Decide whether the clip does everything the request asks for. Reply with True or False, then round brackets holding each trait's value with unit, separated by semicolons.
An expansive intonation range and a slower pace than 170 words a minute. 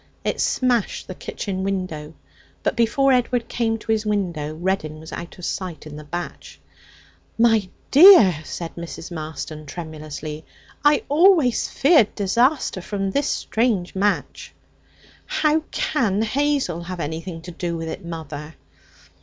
True (6.4 semitones; 135 wpm)